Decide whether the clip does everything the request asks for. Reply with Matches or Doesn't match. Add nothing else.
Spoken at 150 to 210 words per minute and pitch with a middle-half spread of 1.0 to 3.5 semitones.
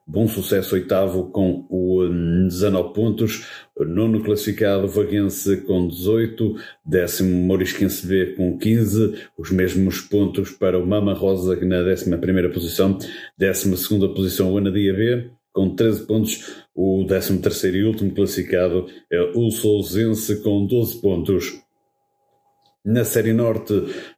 Doesn't match